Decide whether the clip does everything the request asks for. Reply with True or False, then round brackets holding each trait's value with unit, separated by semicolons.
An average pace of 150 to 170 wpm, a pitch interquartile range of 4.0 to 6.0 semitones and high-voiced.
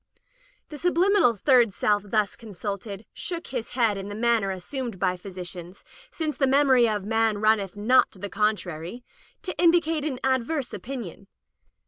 True (160 wpm; 5.1 semitones; 225 Hz)